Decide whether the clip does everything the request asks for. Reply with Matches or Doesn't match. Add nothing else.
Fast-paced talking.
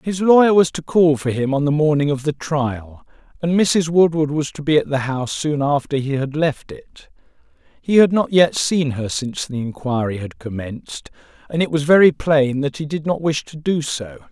Matches